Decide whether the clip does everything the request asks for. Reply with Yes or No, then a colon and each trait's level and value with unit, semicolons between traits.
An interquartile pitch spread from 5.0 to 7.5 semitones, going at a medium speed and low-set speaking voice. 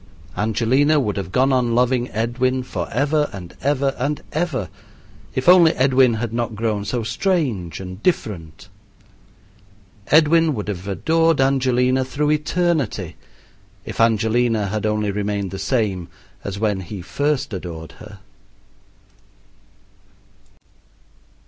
No: average, 5.3 semitones; slow, 115 wpm; low, 120 Hz